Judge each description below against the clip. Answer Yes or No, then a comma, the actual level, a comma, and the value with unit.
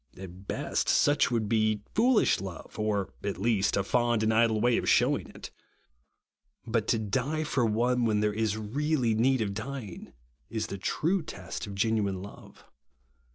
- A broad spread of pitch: No, average, 3.2 semitones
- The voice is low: Yes, low, 110 Hz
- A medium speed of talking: Yes, average, 165 wpm